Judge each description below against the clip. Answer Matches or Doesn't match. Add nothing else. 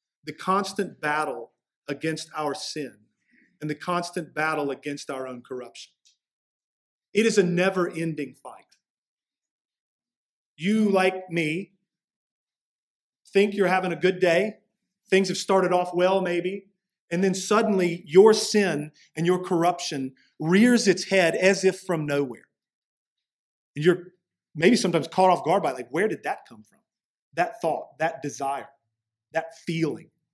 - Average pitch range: Matches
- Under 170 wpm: Matches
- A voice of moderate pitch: Matches